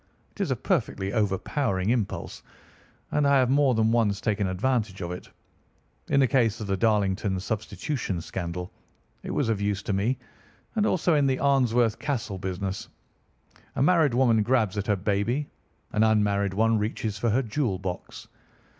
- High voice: No, low, 110 Hz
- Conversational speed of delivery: Yes, average, 165 wpm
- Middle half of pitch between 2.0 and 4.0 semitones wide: No, average, 4.6 semitones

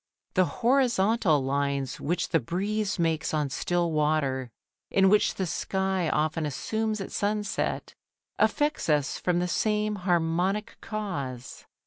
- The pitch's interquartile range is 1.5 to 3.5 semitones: No, wide, 5.4 semitones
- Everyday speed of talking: No, slow, 125 wpm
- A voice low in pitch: No, medium, 175 Hz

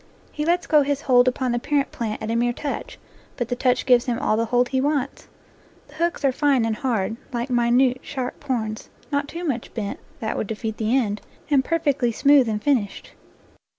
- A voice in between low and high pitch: No, very high, 250 Hz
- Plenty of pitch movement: No, average, 3.6 semitones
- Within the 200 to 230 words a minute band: Yes, fast, 205 wpm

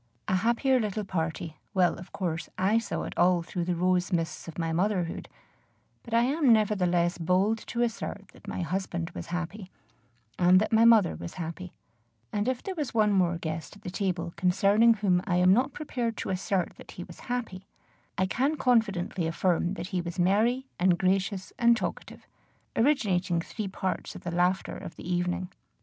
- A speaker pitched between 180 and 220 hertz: Yes, medium, 185 Hz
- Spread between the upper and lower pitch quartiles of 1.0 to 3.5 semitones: No, average, 3.9 semitones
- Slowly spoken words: No, average, 185 wpm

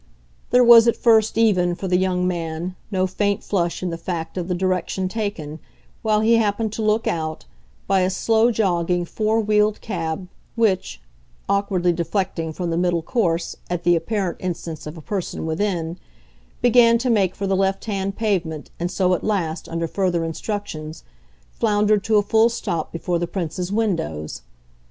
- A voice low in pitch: No, medium, 185 Hz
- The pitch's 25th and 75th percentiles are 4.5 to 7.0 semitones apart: No, average, 3.8 semitones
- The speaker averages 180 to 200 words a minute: No, average, 170 wpm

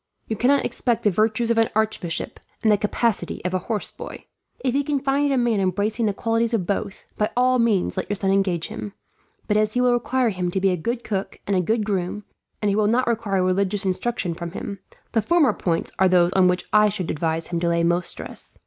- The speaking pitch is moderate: No, high, 210 Hz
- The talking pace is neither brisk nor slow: No, fast, 235 wpm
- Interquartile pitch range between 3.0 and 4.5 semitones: Yes, average, 4.0 semitones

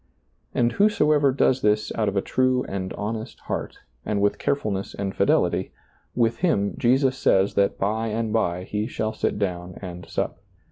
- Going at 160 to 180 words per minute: Yes, average, 170 wpm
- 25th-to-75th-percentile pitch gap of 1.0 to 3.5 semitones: No, average, 4.3 semitones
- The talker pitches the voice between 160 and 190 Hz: No, low, 105 Hz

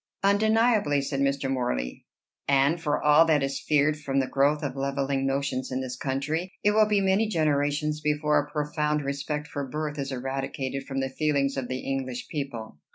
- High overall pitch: No, medium, 140 Hz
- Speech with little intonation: Yes, narrow, 2.0 semitones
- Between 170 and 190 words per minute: Yes, average, 180 wpm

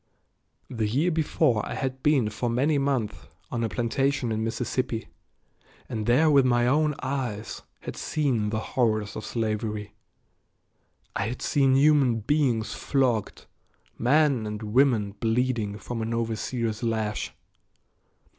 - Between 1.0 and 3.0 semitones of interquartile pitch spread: No, average, 3.6 semitones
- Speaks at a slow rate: Yes, slow, 130 wpm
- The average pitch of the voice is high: No, low, 120 Hz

